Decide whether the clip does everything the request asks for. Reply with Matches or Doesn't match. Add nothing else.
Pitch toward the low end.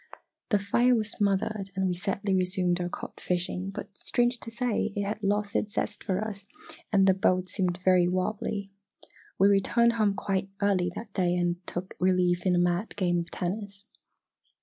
Doesn't match